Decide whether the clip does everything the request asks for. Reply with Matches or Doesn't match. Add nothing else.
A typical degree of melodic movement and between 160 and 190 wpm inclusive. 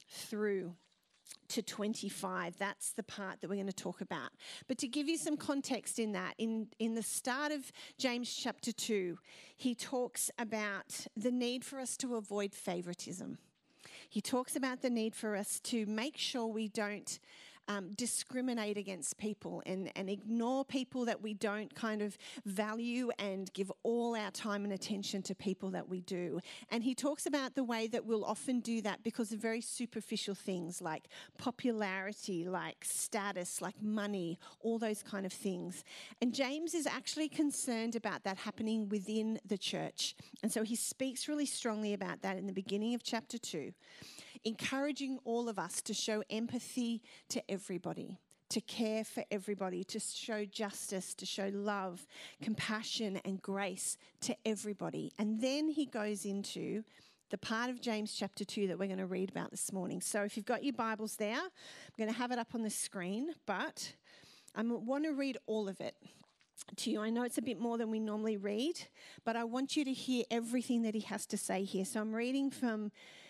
Matches